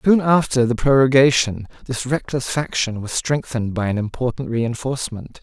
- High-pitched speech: No, low, 125 Hz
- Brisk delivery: No, average, 145 wpm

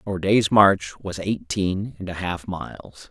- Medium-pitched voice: No, very low, 95 Hz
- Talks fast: No, average, 175 wpm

